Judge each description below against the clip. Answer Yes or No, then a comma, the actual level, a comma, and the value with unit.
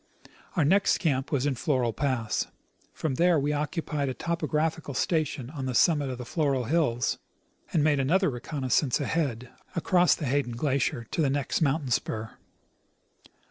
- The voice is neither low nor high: Yes, medium, 145 Hz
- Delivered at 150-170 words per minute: Yes, average, 155 wpm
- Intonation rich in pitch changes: No, average, 3.6 semitones